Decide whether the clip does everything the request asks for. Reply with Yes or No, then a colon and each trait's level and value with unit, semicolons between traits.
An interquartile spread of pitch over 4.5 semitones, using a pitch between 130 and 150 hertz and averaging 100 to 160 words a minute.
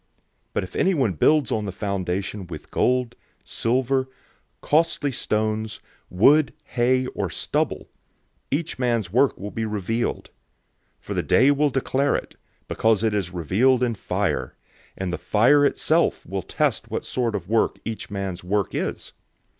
No: average, 4.9 semitones; low, 115 Hz; average, 155 wpm